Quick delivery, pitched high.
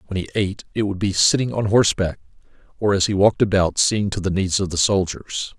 No: fast, 225 wpm; low, 100 Hz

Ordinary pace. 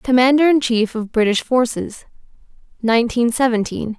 No: slow, 120 wpm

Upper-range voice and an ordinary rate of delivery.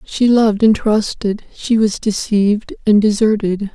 Yes: high, 210 Hz; average, 145 wpm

